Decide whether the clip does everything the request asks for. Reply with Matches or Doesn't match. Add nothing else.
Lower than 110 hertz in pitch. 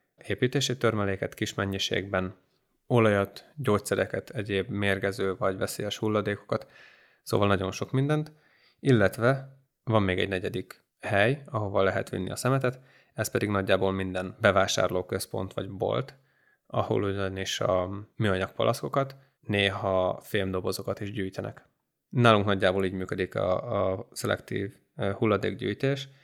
Matches